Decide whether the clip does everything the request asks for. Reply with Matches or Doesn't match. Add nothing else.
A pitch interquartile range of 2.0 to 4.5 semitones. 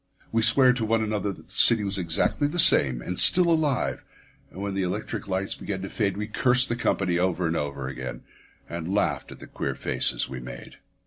Doesn't match